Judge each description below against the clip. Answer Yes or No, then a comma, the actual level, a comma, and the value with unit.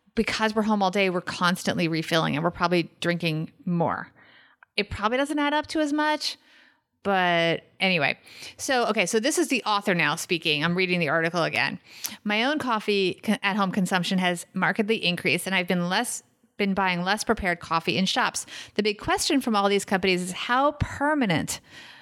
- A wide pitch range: No, average, 4.7 semitones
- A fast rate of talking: No, average, 180 wpm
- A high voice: Yes, high, 195 Hz